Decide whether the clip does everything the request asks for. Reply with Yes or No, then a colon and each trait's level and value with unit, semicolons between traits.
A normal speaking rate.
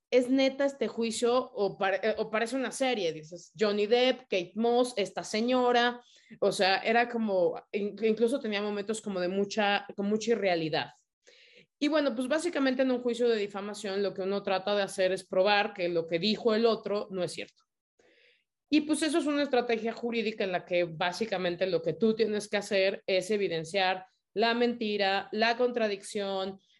Yes: average, 175 wpm